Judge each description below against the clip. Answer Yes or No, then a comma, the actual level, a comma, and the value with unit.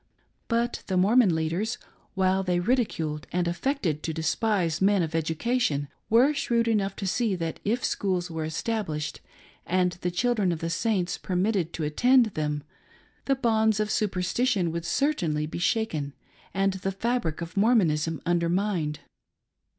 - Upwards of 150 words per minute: No, average, 145 wpm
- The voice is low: No, medium, 185 Hz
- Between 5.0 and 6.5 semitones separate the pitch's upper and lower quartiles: Yes, average, 5.3 semitones